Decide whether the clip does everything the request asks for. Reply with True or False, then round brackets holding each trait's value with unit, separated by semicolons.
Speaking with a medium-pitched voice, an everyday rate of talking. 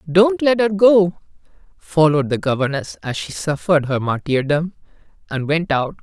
True (165 Hz; 150 wpm)